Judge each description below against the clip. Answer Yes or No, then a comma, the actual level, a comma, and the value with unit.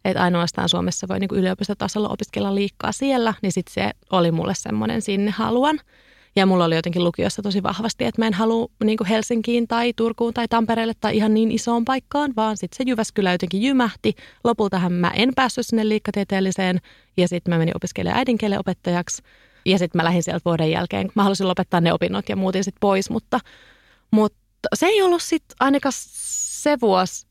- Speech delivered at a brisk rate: Yes, fast, 180 wpm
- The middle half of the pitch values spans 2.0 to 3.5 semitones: No, average, 3.9 semitones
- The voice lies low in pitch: No, high, 210 Hz